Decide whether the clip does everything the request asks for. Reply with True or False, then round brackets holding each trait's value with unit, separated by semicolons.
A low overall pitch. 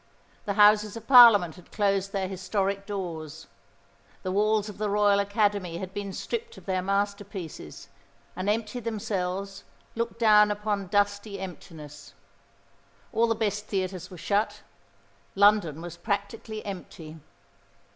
False (200 Hz)